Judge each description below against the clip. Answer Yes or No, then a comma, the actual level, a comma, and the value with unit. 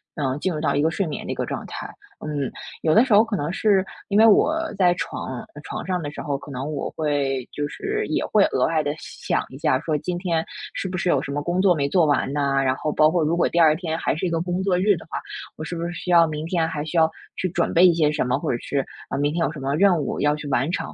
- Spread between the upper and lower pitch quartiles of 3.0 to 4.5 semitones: Yes, average, 3.6 semitones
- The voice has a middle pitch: Yes, medium, 160 Hz